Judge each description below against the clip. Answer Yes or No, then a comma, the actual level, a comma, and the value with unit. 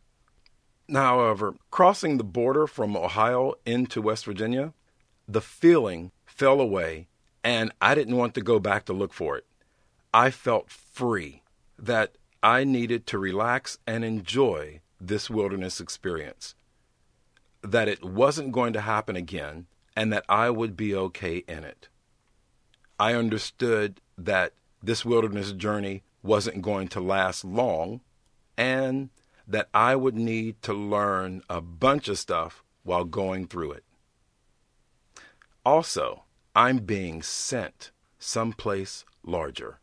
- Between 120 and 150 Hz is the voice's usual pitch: No, low, 110 Hz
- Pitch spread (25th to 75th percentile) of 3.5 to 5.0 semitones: Yes, average, 4.0 semitones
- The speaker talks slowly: Yes, slow, 130 wpm